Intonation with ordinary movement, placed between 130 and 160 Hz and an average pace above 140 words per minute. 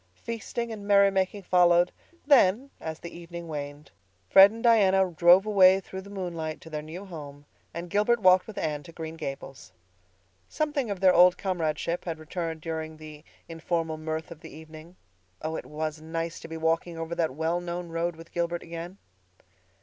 No: average, 3.0 semitones; medium, 170 Hz; average, 180 wpm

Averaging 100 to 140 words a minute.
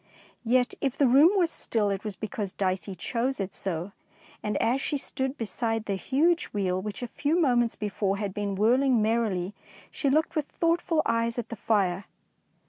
No: average, 185 wpm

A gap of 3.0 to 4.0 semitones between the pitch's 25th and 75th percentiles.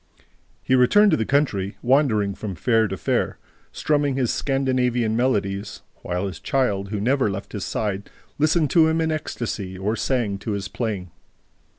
No: average, 5.3 semitones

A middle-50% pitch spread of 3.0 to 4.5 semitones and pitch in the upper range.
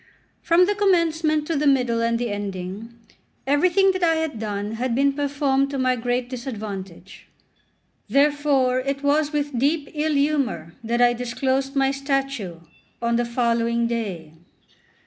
Yes: average, 3.9 semitones; very high, 265 Hz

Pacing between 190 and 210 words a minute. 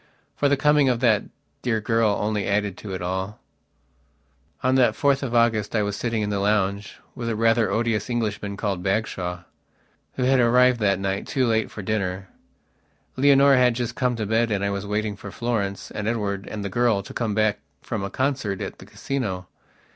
Yes: average, 195 wpm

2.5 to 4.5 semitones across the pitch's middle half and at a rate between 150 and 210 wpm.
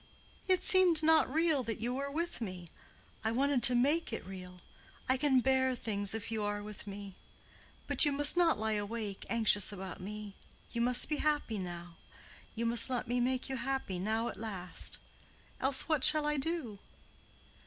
No: average, 5.3 semitones; average, 175 wpm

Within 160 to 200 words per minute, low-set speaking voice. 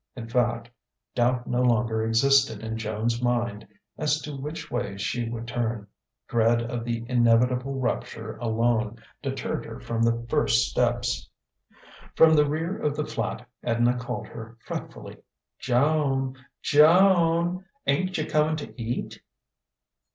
No: slow, 135 wpm; low, 120 Hz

